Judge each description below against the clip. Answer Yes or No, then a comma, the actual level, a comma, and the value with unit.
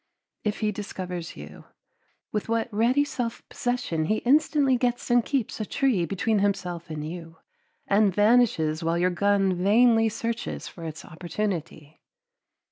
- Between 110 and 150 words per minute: Yes, average, 140 wpm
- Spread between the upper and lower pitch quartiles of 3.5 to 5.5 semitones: Yes, average, 5.2 semitones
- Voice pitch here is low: No, high, 205 Hz